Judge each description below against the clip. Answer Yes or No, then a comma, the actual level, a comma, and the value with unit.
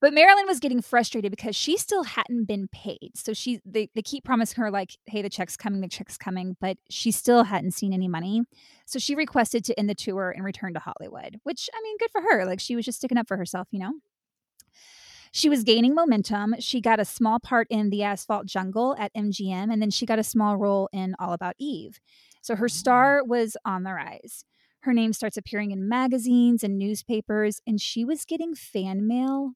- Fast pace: Yes, fast, 215 wpm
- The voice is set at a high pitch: Yes, high, 220 Hz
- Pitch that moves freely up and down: No, average, 3.7 semitones